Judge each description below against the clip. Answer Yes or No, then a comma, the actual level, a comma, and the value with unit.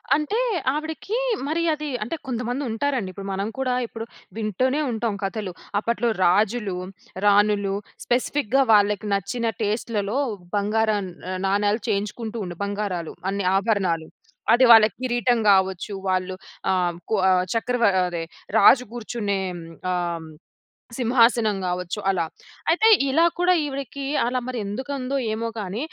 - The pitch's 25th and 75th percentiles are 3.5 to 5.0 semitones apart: Yes, average, 4.0 semitones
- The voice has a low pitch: No, high, 220 Hz